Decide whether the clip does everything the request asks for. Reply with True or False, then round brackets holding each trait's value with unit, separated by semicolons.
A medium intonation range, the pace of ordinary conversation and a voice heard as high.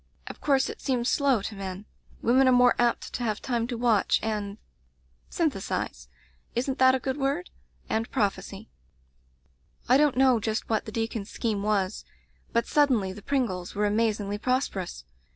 True (4.2 semitones; 175 wpm; 225 Hz)